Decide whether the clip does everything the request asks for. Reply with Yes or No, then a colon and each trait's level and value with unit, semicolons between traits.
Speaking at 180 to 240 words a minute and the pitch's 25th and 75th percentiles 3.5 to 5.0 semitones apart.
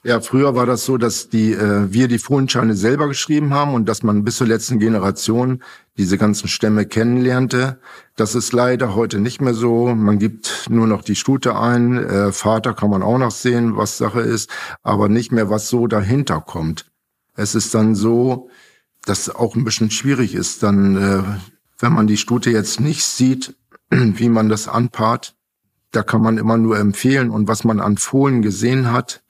No: fast, 190 wpm; average, 2.7 semitones